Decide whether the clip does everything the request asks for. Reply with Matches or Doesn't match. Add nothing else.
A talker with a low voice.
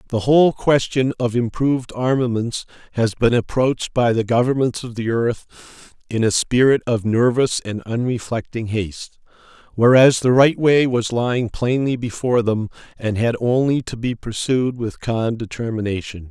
Matches